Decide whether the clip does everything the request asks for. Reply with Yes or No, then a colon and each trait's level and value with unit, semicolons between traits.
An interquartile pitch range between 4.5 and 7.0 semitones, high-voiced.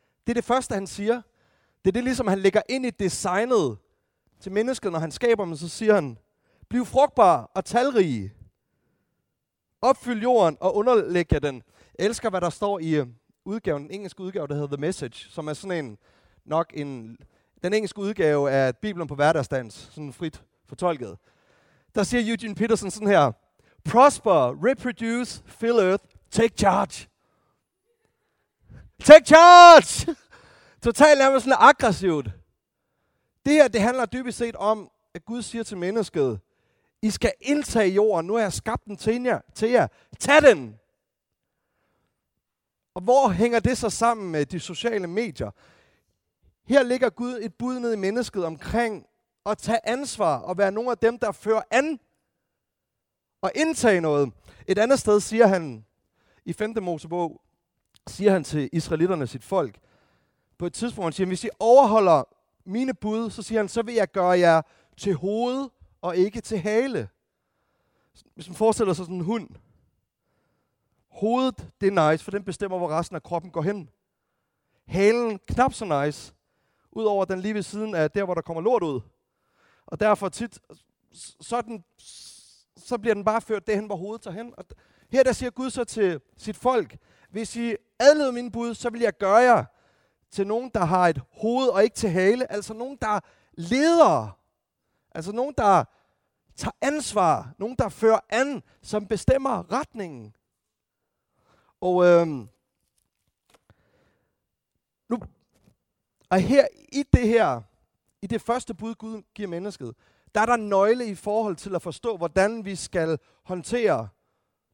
Yes: wide, 5.5 semitones; high, 210 Hz